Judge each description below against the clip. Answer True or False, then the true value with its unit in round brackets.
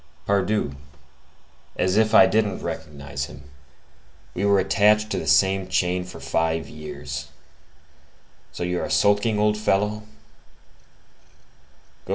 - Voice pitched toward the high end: False (95 Hz)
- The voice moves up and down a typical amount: True (3.2 semitones)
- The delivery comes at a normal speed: False (115 wpm)